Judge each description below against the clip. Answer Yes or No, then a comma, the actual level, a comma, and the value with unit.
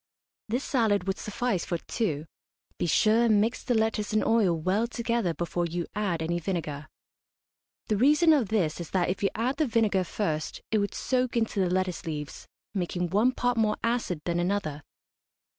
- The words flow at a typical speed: Yes, average, 180 wpm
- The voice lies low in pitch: No, high, 205 Hz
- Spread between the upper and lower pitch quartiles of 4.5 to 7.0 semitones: Yes, average, 4.9 semitones